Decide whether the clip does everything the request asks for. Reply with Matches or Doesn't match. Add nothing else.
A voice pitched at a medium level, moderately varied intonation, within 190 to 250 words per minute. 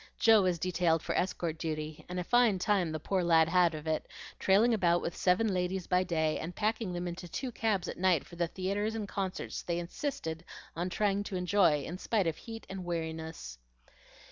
Matches